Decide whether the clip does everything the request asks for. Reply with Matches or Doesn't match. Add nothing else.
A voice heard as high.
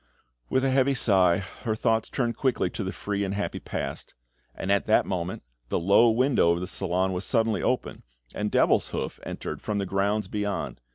Doesn't match